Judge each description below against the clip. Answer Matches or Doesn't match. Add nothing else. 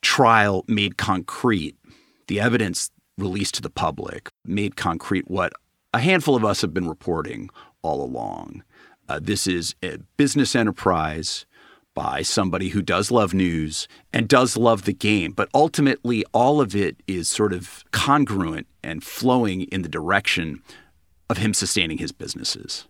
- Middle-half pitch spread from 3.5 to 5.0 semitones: Matches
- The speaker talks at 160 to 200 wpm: Doesn't match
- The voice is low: Matches